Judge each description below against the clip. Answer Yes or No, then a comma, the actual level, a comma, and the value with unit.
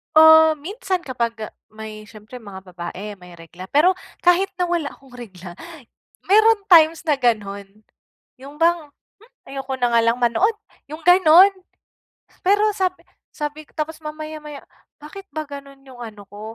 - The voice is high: Yes, very high, 285 Hz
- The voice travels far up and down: Yes, wide, 7.8 semitones